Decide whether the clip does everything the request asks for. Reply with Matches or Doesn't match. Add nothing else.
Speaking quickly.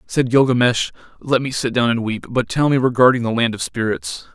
Matches